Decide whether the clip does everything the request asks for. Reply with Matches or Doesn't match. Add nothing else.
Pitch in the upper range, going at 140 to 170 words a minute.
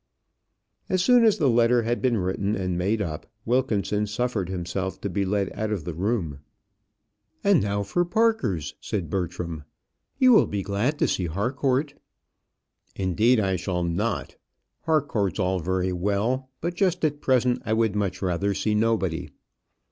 Doesn't match